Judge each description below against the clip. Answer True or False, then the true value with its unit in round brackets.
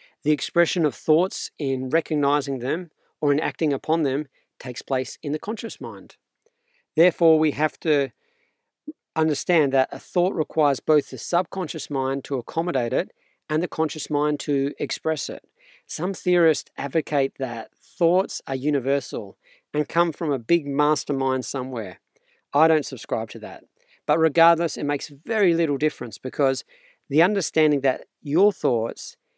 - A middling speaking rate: True (150 wpm)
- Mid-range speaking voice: True (155 Hz)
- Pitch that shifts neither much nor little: True (3.5 semitones)